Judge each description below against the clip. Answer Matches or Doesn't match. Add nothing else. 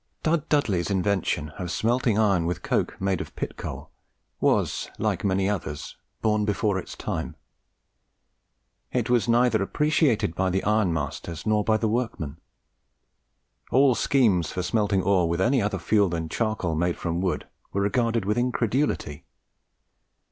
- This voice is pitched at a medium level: Doesn't match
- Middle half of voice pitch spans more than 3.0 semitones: Matches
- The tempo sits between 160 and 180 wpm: Doesn't match